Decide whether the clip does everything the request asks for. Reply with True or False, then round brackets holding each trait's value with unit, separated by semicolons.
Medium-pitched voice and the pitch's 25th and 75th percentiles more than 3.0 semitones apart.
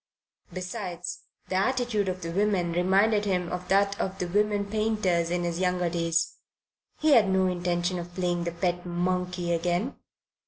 False (180 Hz; 2.4 semitones)